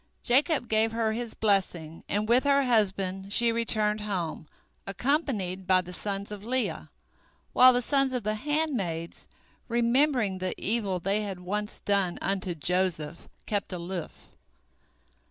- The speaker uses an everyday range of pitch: Yes, average, 4.3 semitones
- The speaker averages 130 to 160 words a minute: Yes, slow, 135 wpm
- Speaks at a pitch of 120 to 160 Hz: No, high, 210 Hz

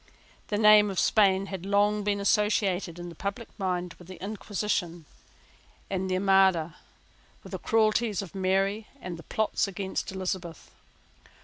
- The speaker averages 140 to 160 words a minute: Yes, average, 145 wpm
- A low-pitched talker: No, high, 195 Hz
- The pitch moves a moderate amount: No, narrow, 2.2 semitones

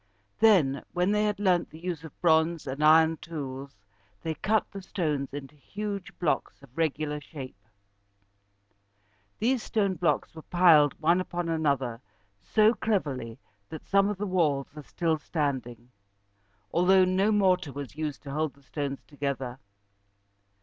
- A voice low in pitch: No, medium, 160 Hz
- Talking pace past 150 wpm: No, average, 145 wpm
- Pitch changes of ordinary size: Yes, average, 4.7 semitones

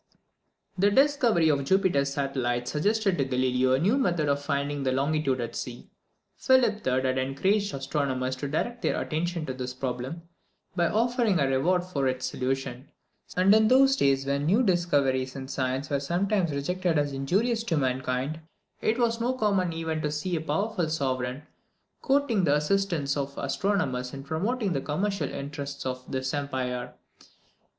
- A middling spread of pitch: No, wide, 6.4 semitones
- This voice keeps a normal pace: Yes, average, 160 wpm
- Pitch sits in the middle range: Yes, medium, 145 Hz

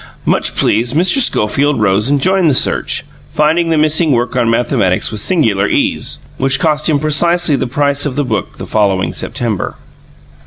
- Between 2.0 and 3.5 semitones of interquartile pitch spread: No, average, 5.1 semitones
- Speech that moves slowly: No, average, 170 wpm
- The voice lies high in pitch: No, medium, 140 Hz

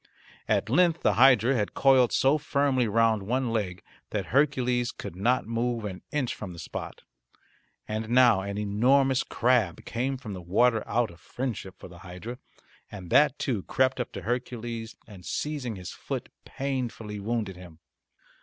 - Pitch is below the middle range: Yes, low, 115 Hz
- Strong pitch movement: No, average, 4.0 semitones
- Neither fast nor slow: Yes, average, 165 wpm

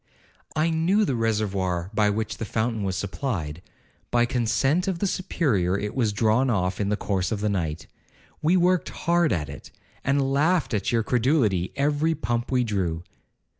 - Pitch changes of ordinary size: No, wide, 6.5 semitones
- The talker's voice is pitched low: Yes, low, 115 Hz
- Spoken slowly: No, average, 170 wpm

